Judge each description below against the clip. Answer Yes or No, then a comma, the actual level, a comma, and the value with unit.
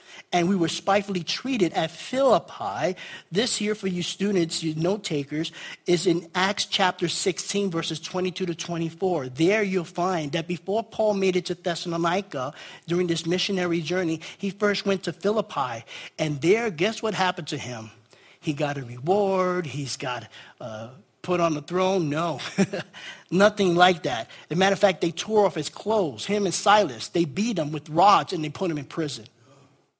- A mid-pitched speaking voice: Yes, medium, 180 Hz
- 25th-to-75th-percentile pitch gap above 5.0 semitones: No, average, 3.3 semitones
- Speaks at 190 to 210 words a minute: No, average, 180 wpm